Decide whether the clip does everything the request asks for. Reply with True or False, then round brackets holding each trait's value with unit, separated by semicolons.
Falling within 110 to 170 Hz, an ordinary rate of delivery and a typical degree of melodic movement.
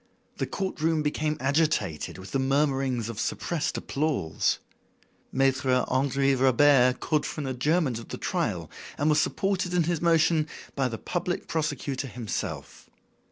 True (140 Hz; 145 wpm; 3.3 semitones)